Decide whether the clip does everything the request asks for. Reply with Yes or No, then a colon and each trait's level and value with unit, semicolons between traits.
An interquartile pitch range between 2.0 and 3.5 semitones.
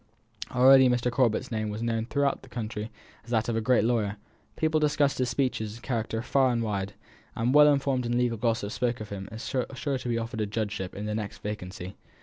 Yes: average, 2.9 semitones